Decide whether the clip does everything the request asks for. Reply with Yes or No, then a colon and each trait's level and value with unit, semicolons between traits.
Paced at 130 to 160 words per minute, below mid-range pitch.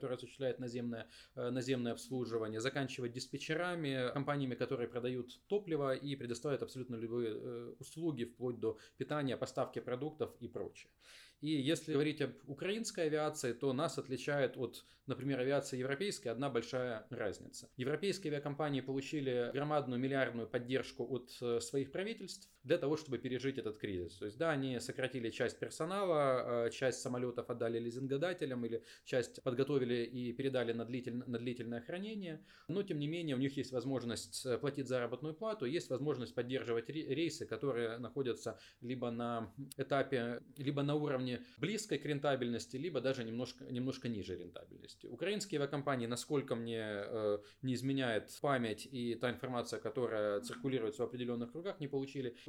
Yes: average, 140 wpm; low, 130 Hz